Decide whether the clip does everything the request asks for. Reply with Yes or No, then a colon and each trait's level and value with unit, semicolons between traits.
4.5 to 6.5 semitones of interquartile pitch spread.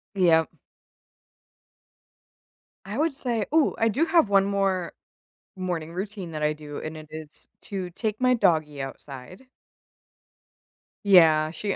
Yes: average, 5.1 semitones